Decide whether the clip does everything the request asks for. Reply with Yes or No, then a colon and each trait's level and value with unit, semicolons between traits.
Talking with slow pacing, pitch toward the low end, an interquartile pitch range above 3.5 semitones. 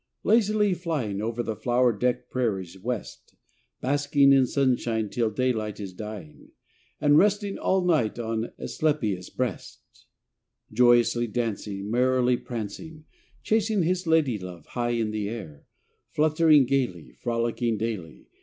Yes: slow, 125 wpm; low, 120 Hz; average, 5.3 semitones